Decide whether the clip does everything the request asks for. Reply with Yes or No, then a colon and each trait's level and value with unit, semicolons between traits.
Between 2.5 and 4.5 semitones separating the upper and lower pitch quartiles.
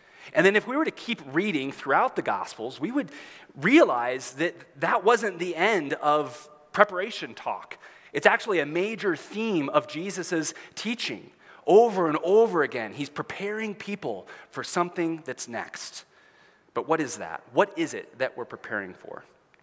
No: wide, 5.6 semitones